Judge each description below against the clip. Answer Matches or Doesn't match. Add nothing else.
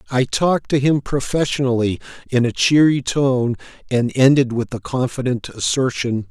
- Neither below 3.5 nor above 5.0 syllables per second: Matches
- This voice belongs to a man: Matches